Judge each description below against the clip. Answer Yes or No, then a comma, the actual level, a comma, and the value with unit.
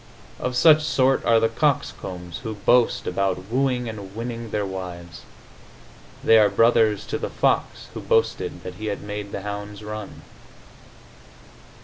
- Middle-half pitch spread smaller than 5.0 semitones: Yes, average, 3.2 semitones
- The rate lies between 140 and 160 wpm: Yes, average, 145 wpm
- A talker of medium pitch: No, low, 105 Hz